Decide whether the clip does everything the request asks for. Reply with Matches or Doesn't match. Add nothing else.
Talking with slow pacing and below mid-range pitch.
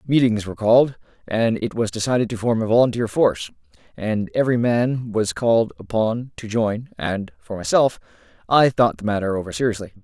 Doesn't match